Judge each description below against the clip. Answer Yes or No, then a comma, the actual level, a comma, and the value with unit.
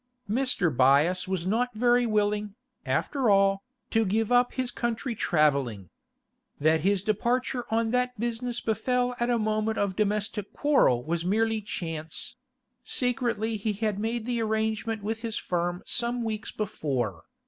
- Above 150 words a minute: No, average, 145 wpm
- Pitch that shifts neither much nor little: Yes, average, 4.0 semitones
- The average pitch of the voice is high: Yes, high, 215 Hz